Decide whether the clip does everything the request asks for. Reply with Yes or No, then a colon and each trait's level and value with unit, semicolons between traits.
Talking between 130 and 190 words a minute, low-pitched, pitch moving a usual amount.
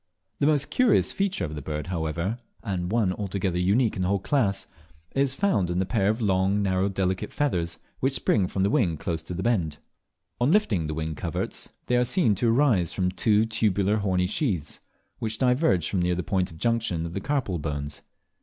No: average, 200 wpm; very low, 95 Hz; average, 4.8 semitones